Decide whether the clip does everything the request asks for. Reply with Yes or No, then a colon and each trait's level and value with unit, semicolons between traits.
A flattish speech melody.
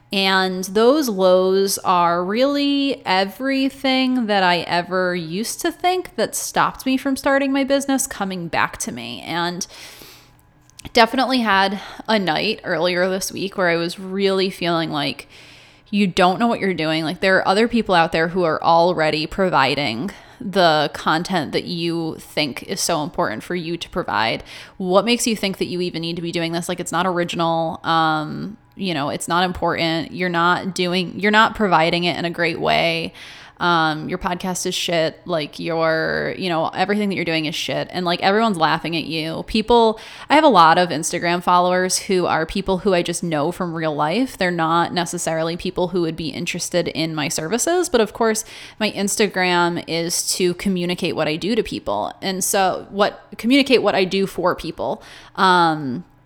No: average, 3.3 semitones